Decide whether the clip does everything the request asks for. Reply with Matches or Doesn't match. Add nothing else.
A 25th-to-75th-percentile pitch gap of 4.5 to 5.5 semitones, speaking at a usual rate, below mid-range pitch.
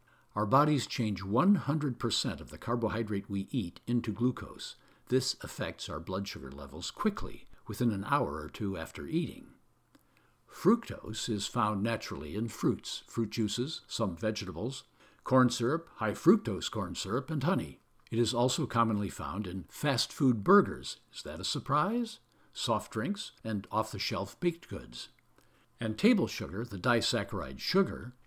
Doesn't match